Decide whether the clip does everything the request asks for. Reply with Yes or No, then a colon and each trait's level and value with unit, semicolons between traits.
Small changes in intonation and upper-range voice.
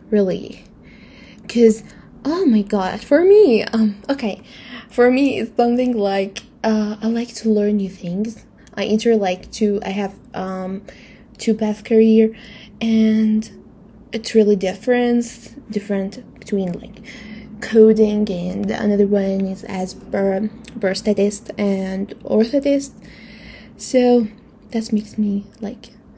Yes: narrow, 2.1 semitones; high, 215 Hz